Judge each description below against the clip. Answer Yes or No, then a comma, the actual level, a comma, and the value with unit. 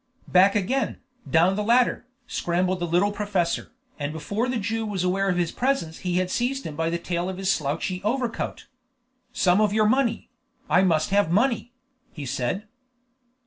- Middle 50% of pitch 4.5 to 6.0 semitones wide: No, average, 4.0 semitones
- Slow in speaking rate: No, average, 175 wpm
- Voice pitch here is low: No, high, 190 Hz